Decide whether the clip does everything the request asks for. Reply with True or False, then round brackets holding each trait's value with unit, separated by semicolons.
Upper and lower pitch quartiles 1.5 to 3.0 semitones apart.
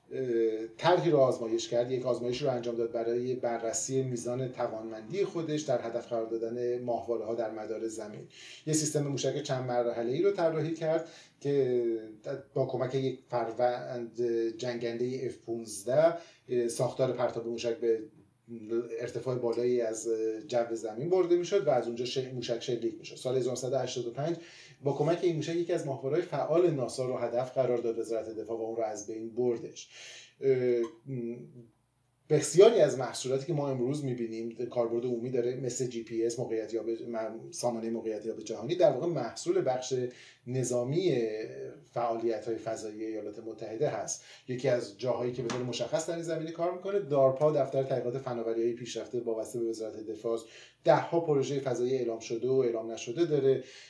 True (2.6 semitones)